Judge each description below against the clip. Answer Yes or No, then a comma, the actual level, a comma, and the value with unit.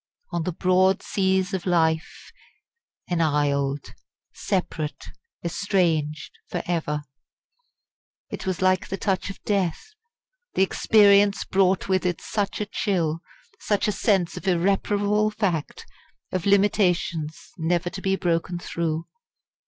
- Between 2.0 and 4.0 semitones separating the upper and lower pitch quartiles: Yes, average, 3.1 semitones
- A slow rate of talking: Yes, slow, 120 wpm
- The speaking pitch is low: No, medium, 185 Hz